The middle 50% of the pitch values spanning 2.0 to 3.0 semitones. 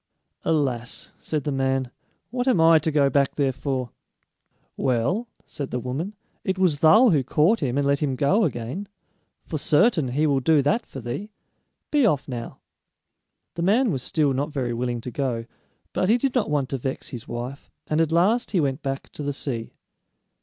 No: average, 4.6 semitones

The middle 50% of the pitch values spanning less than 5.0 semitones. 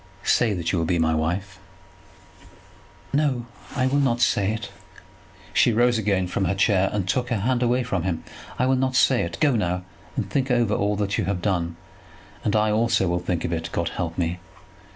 No: wide, 5.4 semitones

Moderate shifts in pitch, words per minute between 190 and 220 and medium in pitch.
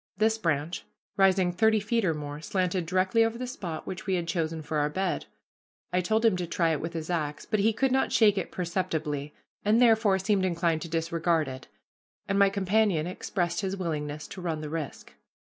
Yes: average, 3.8 semitones; average, 200 wpm; medium, 180 Hz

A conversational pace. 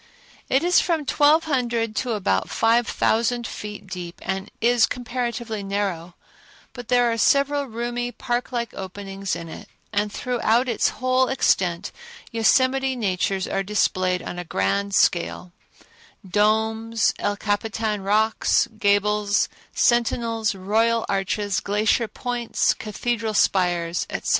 No: slow, 125 wpm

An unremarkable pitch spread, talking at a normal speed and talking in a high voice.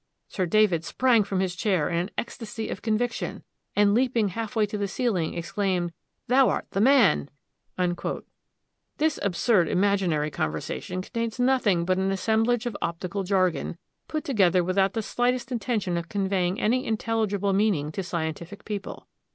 Yes: average, 3.9 semitones; average, 150 wpm; high, 200 Hz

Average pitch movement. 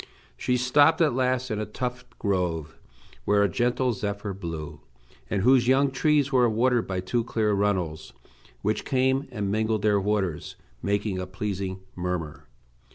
Yes: average, 4.8 semitones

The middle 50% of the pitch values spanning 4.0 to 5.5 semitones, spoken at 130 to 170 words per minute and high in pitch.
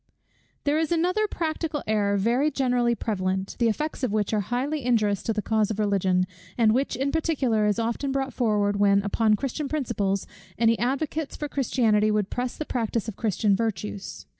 No: average, 4.7 semitones; average, 185 wpm; high, 230 Hz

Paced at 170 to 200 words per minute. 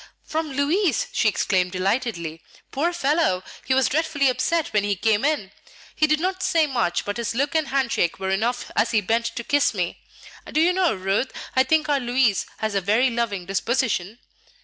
Yes: average, 195 wpm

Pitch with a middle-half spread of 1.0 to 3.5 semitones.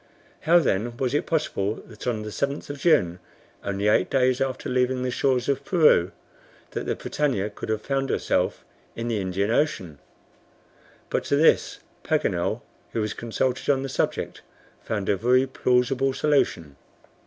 No: average, 4.4 semitones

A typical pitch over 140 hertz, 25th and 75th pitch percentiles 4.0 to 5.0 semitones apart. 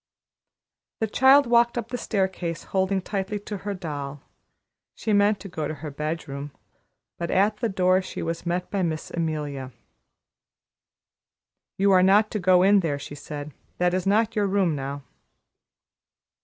Yes: medium, 185 Hz; average, 4.7 semitones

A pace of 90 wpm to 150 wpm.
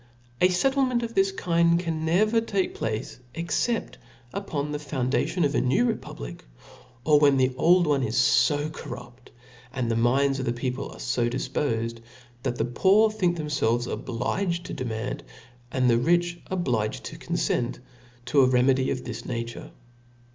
No: average, 160 wpm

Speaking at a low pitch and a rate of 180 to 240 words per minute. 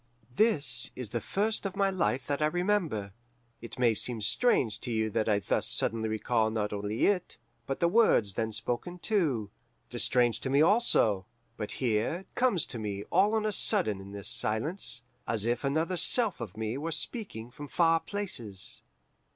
Yes: low, 125 Hz; average, 185 wpm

